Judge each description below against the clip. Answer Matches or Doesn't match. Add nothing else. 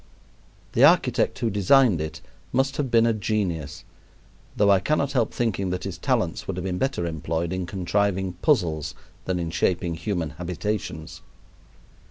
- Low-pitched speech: Matches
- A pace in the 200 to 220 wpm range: Doesn't match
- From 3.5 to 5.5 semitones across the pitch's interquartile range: Matches